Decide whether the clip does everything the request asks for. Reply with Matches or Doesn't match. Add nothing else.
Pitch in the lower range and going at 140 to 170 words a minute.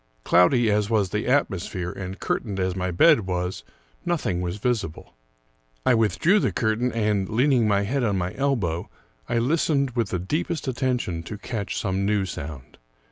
Matches